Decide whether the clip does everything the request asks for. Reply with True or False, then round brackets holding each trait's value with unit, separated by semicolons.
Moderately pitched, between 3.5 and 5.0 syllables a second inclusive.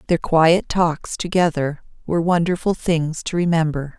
True (165 Hz; 4.5 syllables/s)